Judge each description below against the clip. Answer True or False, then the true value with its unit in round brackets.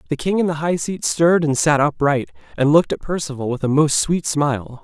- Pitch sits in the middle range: True (150 Hz)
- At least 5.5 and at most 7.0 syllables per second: True (5.8 syllables/s)